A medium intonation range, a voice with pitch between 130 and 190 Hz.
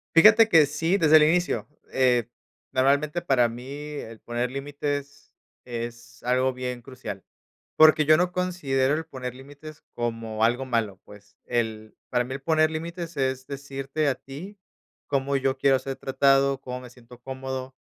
Yes: average, 3.4 semitones; low, 135 Hz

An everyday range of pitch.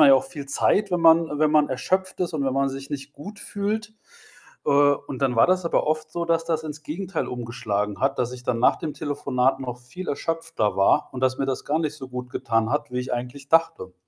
Yes: average, 4.4 semitones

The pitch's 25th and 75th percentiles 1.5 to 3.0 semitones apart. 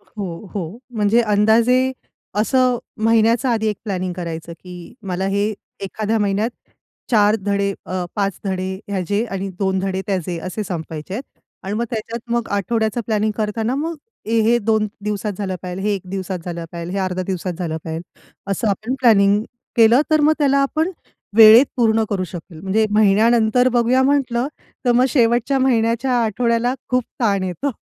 No: average, 3.7 semitones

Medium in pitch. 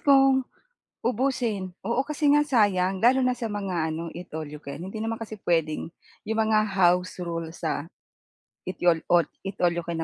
No: high, 195 Hz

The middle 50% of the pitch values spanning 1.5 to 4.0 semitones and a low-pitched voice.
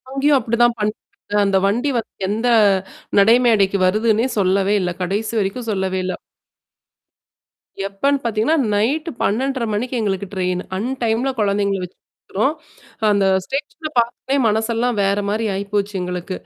No: average, 3.5 semitones; high, 215 Hz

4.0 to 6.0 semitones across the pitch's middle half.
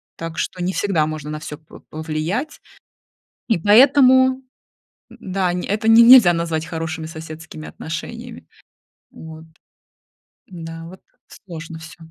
Yes: average, 4.9 semitones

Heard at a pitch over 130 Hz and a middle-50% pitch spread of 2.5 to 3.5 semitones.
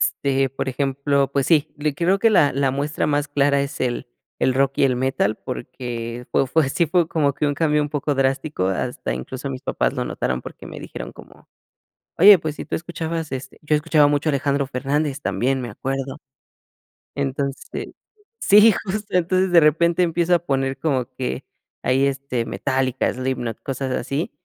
Yes: medium, 140 Hz; average, 2.8 semitones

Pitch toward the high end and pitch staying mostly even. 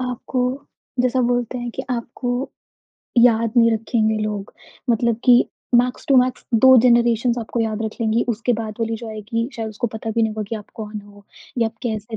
Yes: high, 230 Hz; narrow, 1.9 semitones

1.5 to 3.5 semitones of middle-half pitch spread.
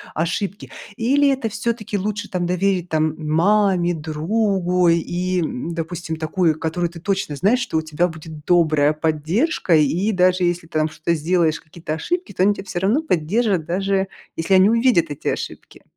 No: average, 3.9 semitones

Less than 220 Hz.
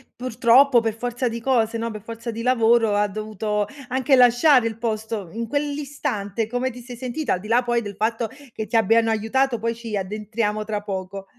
No: high, 230 Hz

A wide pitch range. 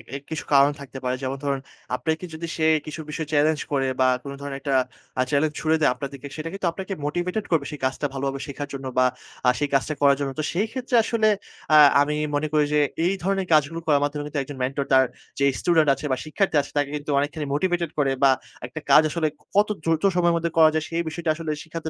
No: average, 2.8 semitones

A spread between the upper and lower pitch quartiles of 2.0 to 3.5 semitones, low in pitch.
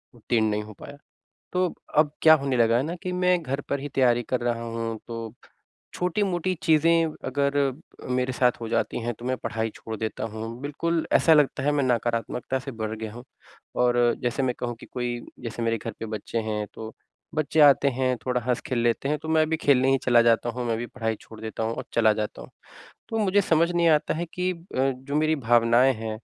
No: average, 4.4 semitones; low, 125 Hz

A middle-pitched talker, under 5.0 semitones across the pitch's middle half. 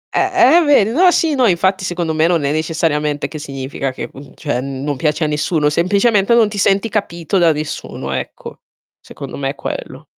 No: medium, 165 Hz; wide, 5.6 semitones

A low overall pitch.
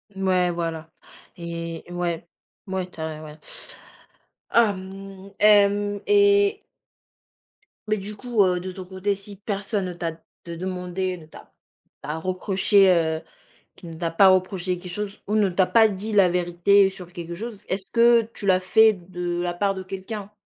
No: medium, 185 Hz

